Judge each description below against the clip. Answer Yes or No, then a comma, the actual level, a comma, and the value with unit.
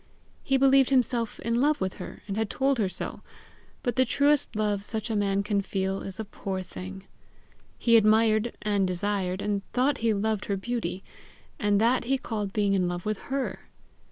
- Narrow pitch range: No, average, 3.5 semitones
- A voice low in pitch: No, high, 215 Hz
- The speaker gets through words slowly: No, average, 185 wpm